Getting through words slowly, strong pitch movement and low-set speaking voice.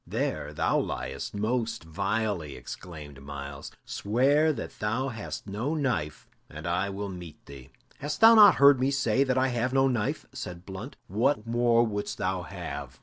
No: average, 165 wpm; wide, 7.0 semitones; low, 105 Hz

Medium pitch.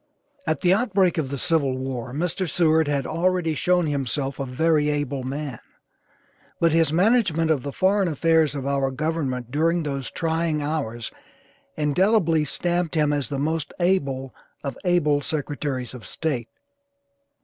Yes: medium, 150 Hz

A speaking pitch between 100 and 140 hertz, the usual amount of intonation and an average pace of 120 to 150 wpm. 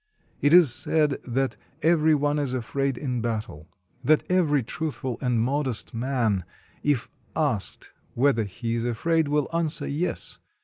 Yes: low, 135 Hz; average, 4.2 semitones; average, 140 wpm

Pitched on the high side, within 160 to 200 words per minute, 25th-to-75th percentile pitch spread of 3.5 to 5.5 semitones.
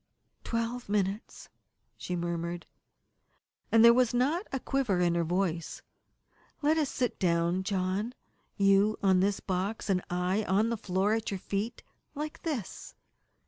No: high, 200 Hz; average, 140 wpm; average, 4.3 semitones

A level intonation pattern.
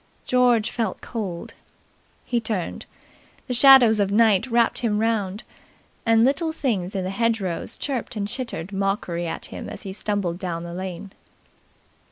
No: average, 3.7 semitones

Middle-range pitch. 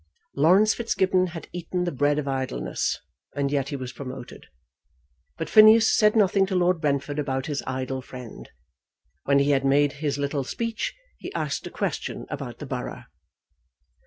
Yes: medium, 145 Hz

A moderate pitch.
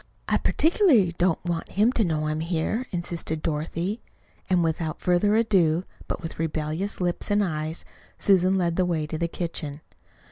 Yes: medium, 170 Hz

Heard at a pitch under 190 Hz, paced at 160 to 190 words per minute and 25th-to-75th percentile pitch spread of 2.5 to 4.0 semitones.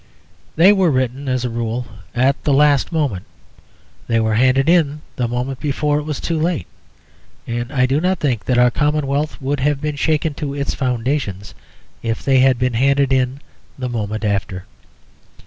Yes: low, 135 Hz; average, 175 wpm; average, 3.4 semitones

